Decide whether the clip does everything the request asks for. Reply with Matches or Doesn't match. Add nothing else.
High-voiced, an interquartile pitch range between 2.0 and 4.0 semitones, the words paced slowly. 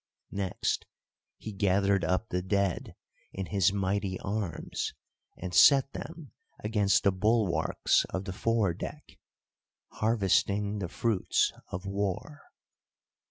Doesn't match